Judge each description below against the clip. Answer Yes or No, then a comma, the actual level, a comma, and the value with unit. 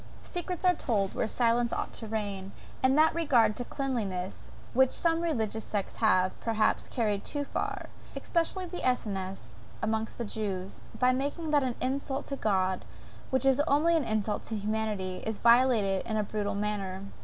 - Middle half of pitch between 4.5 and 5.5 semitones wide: Yes, average, 4.9 semitones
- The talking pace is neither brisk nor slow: Yes, average, 165 wpm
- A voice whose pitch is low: No, high, 225 Hz